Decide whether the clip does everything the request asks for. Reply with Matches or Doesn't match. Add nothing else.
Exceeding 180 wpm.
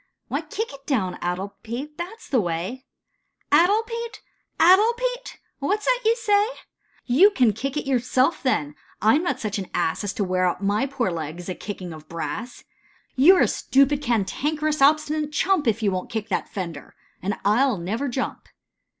Matches